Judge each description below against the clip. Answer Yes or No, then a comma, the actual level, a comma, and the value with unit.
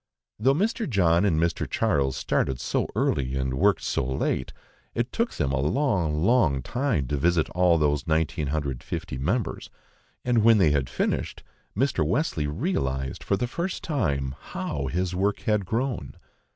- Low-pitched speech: Yes, very low, 85 Hz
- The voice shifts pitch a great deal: Yes, wide, 8.6 semitones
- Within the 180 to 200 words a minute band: No, average, 155 wpm